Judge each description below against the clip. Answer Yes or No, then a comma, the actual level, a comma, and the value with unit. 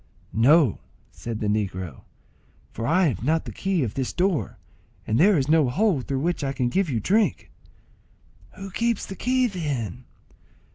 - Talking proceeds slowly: No, average, 170 wpm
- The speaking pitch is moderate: Yes, medium, 150 Hz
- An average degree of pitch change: No, wide, 8.0 semitones